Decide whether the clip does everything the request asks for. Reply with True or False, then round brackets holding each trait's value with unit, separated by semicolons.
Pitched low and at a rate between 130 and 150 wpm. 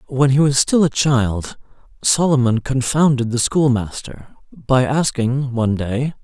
True (130 Hz; 135 wpm)